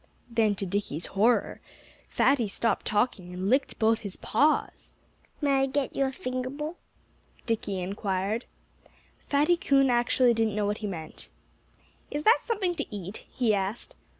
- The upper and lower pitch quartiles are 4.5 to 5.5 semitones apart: Yes, average, 5.2 semitones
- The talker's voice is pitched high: Yes, high, 230 Hz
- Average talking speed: Yes, average, 150 wpm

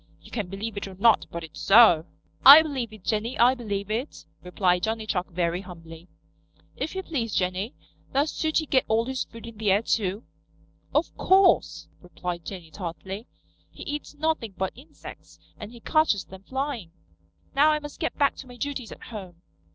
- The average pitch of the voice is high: Yes, high, 220 Hz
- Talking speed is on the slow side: No, average, 180 wpm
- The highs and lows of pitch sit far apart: Yes, wide, 6.1 semitones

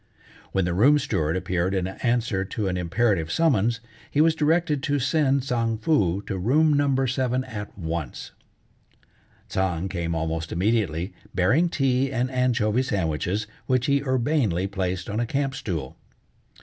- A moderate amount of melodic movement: No, wide, 6.6 semitones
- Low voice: Yes, low, 115 Hz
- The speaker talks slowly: No, average, 150 wpm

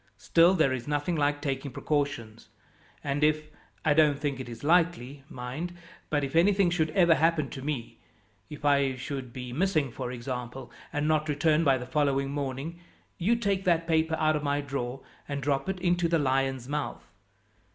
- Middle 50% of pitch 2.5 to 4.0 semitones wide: Yes, average, 3.3 semitones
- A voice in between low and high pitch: Yes, medium, 145 Hz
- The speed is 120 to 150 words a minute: No, average, 180 wpm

